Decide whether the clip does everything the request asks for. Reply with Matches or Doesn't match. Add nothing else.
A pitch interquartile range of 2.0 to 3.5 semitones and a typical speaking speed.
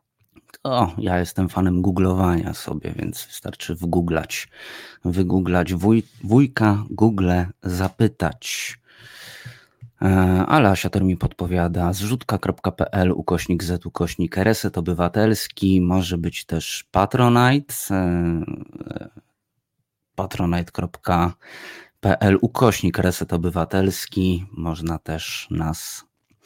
Doesn't match